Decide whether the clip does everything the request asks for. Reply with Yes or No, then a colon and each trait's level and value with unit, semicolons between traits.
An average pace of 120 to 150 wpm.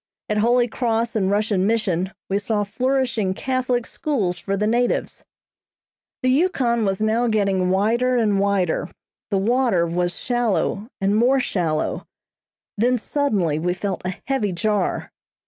Yes: average, 140 wpm